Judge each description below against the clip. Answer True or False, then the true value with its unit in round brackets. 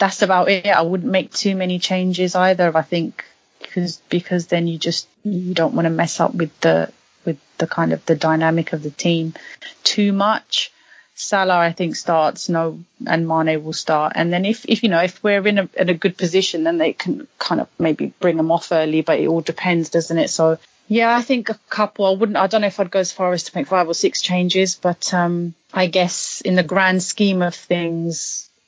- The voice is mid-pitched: True (180 Hz)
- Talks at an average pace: False (225 wpm)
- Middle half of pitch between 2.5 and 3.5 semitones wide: True (2.9 semitones)